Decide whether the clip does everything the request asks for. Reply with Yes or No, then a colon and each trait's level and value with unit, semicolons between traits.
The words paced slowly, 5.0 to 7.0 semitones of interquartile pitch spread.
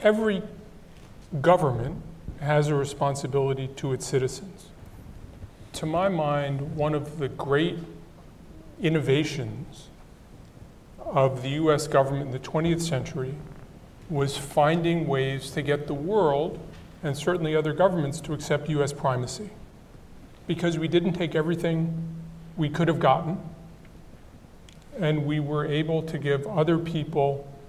No: slow, 120 wpm; average, 2.9 semitones